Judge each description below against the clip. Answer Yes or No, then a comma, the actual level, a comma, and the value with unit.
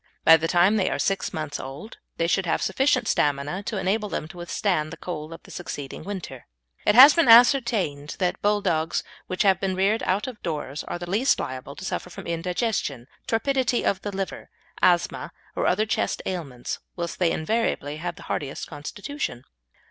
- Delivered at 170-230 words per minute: Yes, average, 185 wpm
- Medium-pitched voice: Yes, medium, 180 Hz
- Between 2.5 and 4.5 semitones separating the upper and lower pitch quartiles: No, average, 5.1 semitones